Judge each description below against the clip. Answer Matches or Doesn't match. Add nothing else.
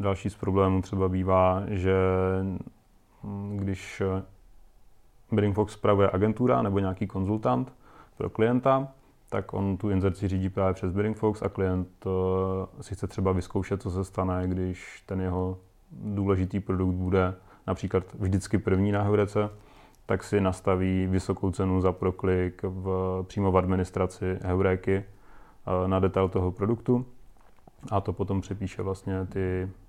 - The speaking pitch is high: Doesn't match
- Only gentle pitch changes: Matches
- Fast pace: Doesn't match